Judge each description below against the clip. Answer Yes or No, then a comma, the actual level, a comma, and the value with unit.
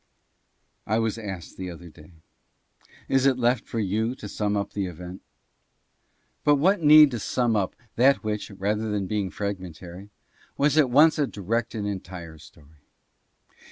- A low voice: Yes, low, 105 Hz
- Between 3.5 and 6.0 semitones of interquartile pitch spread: Yes, average, 4.9 semitones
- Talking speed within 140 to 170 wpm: Yes, average, 160 wpm